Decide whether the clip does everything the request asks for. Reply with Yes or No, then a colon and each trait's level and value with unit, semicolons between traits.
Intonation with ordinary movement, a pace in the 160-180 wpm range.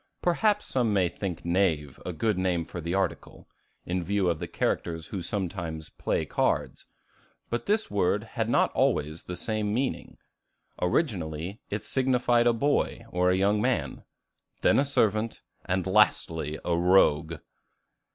No: average, 4.6 semitones; average, 145 wpm